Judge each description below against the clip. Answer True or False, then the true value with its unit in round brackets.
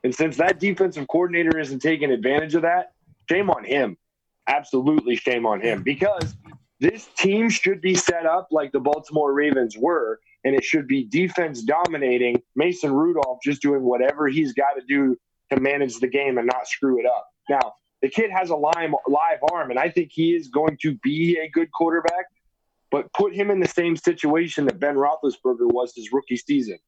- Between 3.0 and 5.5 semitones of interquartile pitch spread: True (5.1 semitones)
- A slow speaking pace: False (190 wpm)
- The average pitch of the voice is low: False (160 Hz)